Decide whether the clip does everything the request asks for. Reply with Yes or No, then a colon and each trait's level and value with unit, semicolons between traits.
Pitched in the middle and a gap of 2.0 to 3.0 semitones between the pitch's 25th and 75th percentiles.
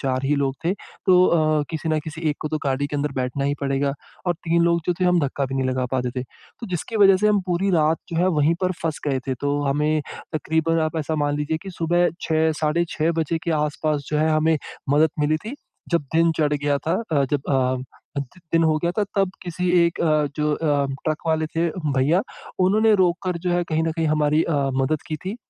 Yes: medium, 155 Hz; average, 2.7 semitones